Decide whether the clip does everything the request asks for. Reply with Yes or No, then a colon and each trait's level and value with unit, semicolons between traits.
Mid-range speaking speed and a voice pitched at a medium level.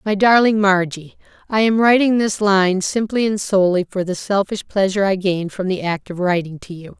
No: average, 195 wpm; high, 195 Hz